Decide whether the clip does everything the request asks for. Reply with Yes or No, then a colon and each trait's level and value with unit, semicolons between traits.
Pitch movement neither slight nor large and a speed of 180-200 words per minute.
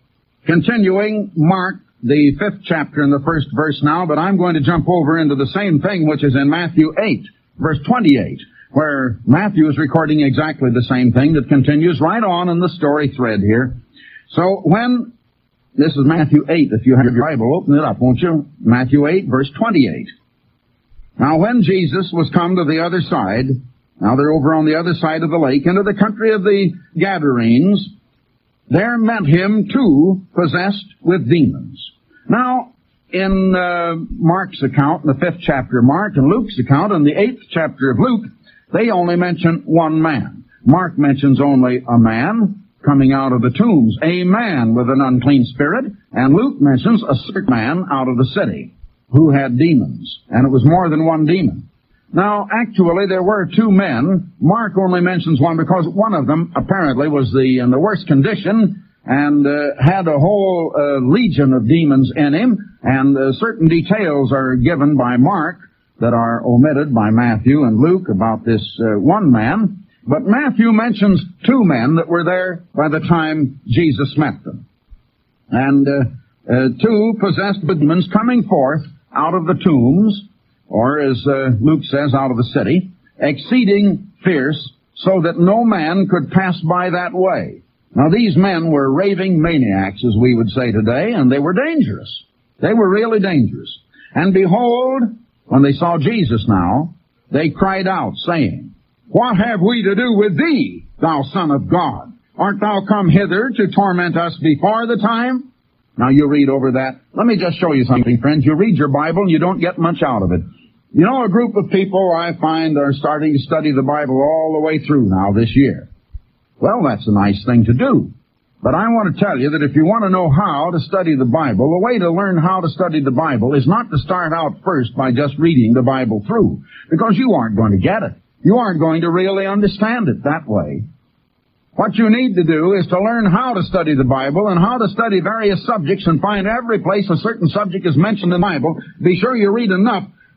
No: wide, 5.9 semitones; average, 190 wpm